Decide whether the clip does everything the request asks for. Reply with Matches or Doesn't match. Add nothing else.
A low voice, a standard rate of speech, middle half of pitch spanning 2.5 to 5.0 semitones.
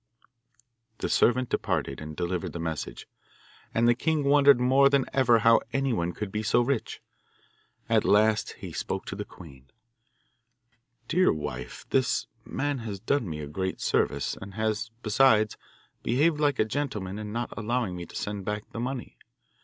Doesn't match